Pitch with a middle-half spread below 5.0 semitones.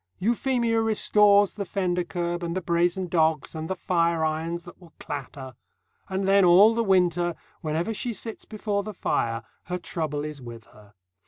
Yes: average, 4.0 semitones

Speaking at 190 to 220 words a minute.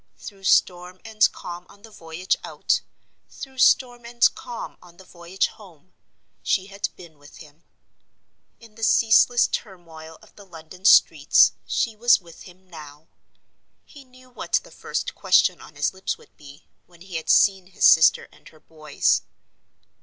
No: average, 160 wpm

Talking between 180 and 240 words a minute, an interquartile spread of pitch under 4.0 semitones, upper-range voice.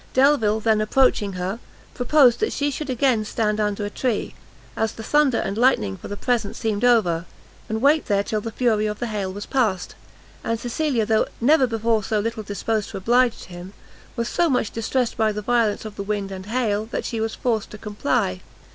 Yes: average, 200 wpm; average, 3.0 semitones; high, 220 Hz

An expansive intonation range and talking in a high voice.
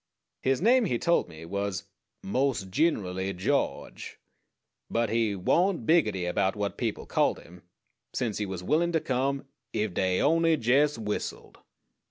No: wide, 7.6 semitones; low, 110 Hz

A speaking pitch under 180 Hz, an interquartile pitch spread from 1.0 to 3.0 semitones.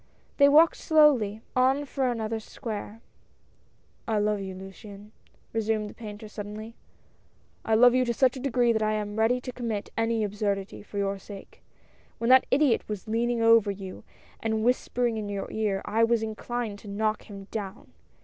No: high, 220 Hz; narrow, 2.6 semitones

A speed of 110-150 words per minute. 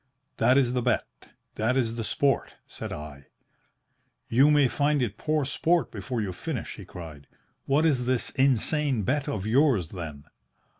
No: average, 160 wpm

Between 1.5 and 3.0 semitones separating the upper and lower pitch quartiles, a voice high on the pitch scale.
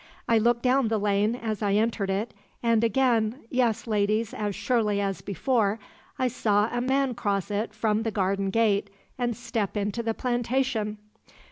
Yes: average, 2.7 semitones; high, 220 Hz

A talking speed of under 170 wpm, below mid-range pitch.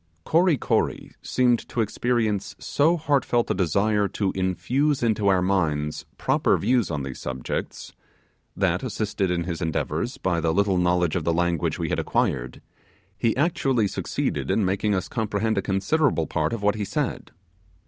Yes: average, 155 wpm; low, 100 Hz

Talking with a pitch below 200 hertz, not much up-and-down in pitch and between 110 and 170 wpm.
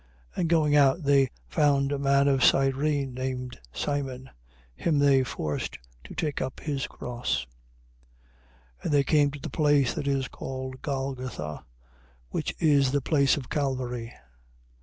Yes: low, 135 Hz; narrow, 1.7 semitones; average, 150 wpm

